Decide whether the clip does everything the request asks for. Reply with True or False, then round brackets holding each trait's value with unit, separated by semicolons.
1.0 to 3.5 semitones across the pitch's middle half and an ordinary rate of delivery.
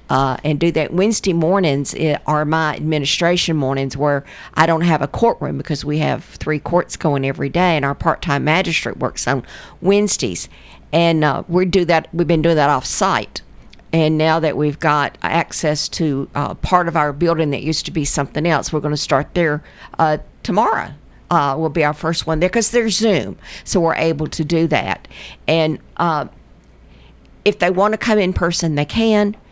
True (2.8 semitones; 190 wpm)